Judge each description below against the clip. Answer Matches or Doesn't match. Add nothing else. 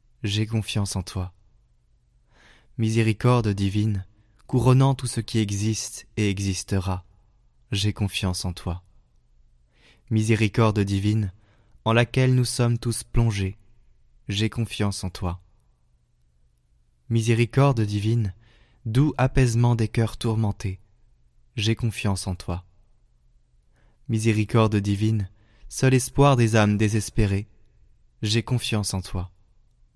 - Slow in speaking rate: Matches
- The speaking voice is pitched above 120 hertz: Doesn't match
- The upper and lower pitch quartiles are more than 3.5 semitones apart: Doesn't match